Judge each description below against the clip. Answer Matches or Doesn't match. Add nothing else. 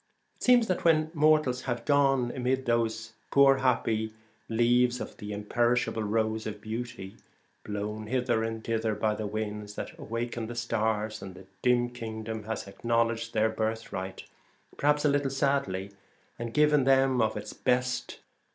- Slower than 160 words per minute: Matches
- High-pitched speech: Doesn't match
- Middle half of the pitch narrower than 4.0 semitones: Matches